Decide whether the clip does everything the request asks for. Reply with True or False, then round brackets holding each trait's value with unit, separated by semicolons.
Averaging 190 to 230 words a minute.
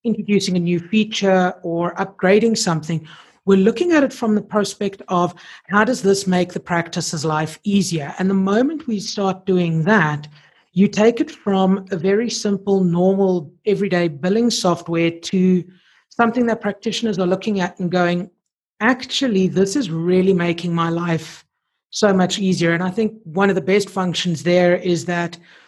False (165 wpm)